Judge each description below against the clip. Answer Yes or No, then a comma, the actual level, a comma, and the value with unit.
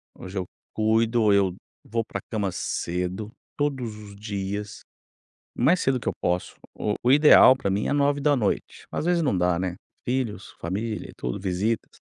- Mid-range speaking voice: No, low, 105 Hz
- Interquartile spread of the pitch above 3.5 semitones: Yes, average, 4.8 semitones